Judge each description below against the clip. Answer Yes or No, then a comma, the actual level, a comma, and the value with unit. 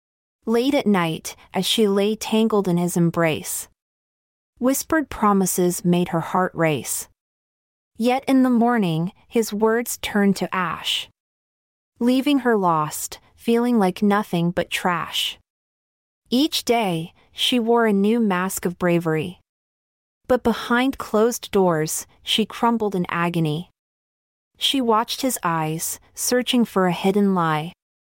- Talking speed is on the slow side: Yes, slow, 125 wpm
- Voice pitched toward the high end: Yes, high, 205 Hz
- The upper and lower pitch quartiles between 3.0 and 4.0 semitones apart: No, average, 5.0 semitones